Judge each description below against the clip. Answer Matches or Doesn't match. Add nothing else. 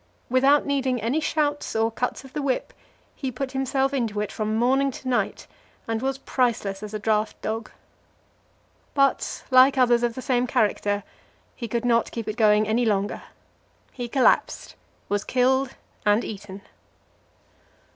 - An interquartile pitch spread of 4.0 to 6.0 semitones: Doesn't match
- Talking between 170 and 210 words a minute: Doesn't match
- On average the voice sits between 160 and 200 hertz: Doesn't match